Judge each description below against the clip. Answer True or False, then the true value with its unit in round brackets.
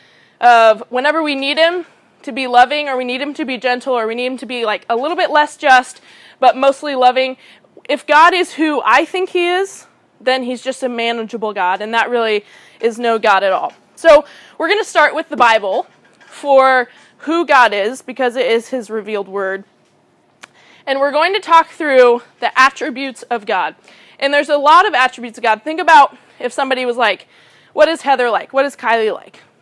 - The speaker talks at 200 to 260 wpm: True (205 wpm)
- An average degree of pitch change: True (4.0 semitones)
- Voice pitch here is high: True (260 Hz)